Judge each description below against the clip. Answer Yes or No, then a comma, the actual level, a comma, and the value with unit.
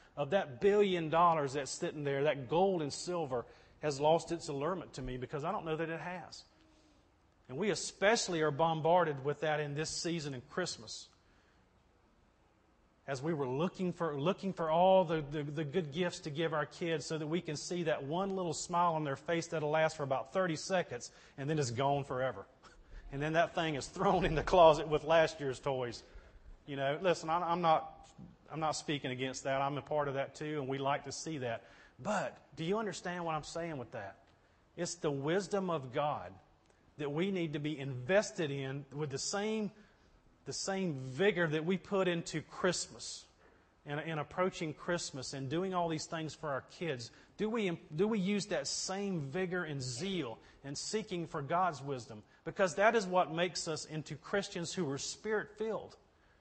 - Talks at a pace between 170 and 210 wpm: Yes, average, 195 wpm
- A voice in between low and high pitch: Yes, medium, 155 Hz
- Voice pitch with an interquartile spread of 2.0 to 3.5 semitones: No, average, 4.4 semitones